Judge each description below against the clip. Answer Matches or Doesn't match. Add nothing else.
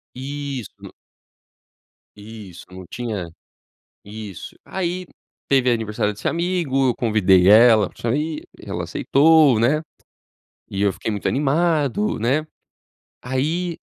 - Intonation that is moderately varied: Doesn't match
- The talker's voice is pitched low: Matches